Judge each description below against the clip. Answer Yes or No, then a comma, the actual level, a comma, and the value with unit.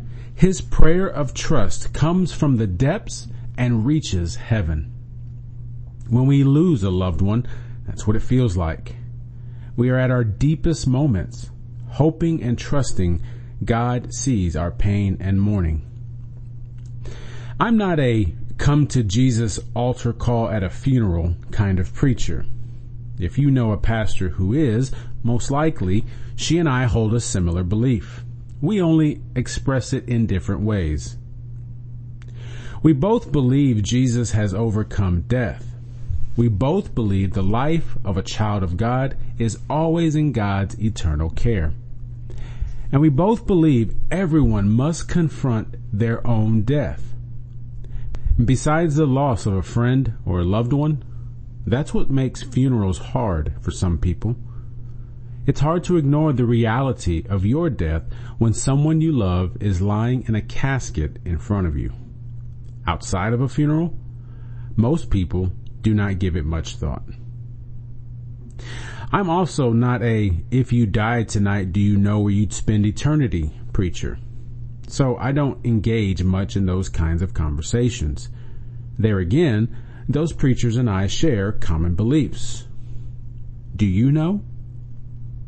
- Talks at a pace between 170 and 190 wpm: No, average, 140 wpm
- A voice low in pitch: Yes, low, 120 Hz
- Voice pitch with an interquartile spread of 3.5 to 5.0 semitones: No, narrow, 2.6 semitones